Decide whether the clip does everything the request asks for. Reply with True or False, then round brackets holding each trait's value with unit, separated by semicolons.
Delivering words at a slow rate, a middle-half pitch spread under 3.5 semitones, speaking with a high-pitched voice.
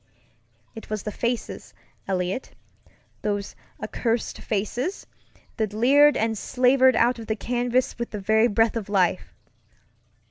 True (130 wpm; 2.8 semitones; 225 Hz)